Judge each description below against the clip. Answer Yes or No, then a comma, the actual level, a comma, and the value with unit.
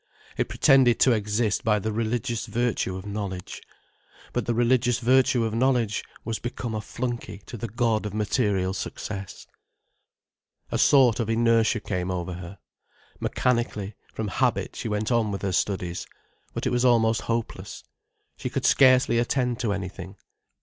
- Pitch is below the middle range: Yes, low, 110 Hz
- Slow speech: No, average, 155 wpm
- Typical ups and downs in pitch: Yes, average, 3.1 semitones